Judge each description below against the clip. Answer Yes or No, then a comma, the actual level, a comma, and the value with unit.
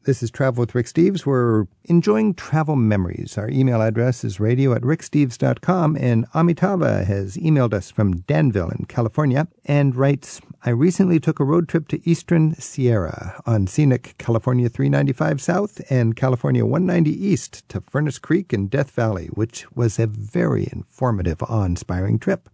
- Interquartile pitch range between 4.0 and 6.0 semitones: Yes, wide, 5.5 semitones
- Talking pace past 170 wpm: No, average, 155 wpm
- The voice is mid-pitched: No, low, 130 Hz